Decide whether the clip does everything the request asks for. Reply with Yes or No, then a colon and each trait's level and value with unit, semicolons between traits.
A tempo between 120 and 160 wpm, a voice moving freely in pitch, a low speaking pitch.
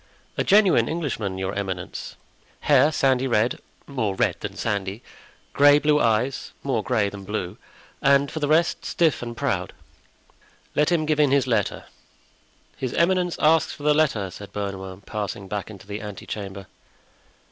Yes: average, 150 wpm; wide, 6.7 semitones; low, 120 Hz